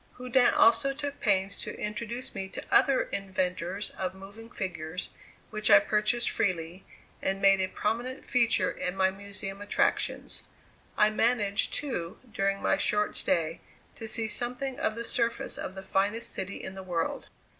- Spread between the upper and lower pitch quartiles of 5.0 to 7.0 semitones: No, average, 3.4 semitones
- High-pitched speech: Yes, high, 205 Hz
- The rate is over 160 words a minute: No, average, 155 wpm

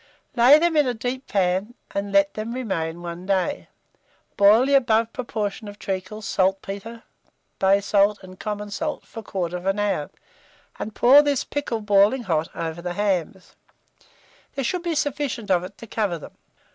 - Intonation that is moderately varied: Yes, average, 4.0 semitones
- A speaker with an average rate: Yes, average, 160 wpm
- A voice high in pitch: Yes, high, 205 Hz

